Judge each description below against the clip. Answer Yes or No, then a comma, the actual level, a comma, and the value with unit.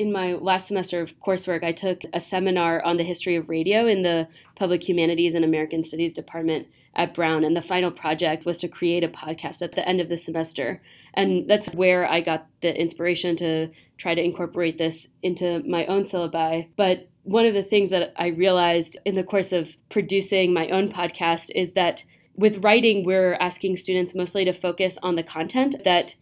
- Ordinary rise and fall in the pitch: No, narrow, 2.0 semitones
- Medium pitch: Yes, medium, 175 Hz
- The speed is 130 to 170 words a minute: No, average, 195 wpm